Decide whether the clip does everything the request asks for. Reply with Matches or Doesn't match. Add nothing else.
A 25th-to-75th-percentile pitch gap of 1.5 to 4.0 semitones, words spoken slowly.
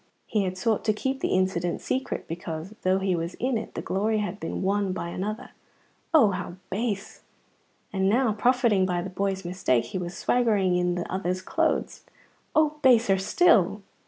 Doesn't match